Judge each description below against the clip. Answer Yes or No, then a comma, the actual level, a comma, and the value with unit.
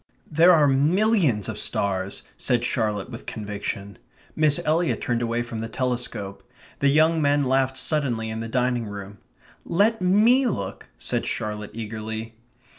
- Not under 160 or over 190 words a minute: No, average, 145 wpm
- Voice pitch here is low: Yes, low, 120 Hz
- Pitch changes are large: Yes, wide, 5.9 semitones